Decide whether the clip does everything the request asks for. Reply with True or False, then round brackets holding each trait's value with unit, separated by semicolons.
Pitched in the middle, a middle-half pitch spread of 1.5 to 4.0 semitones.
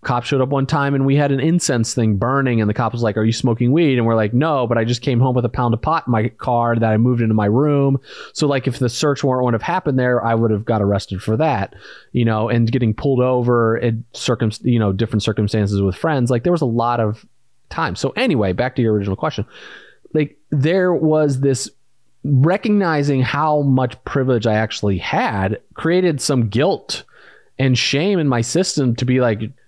False (125 Hz; 3.7 semitones)